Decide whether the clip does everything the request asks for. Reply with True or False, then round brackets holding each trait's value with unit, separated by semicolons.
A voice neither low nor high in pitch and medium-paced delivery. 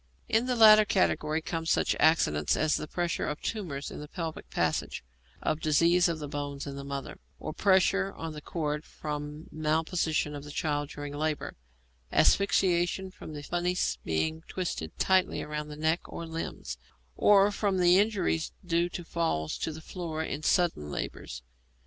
True (160 Hz; 165 wpm)